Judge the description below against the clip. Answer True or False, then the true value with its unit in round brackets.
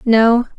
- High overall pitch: True (230 Hz)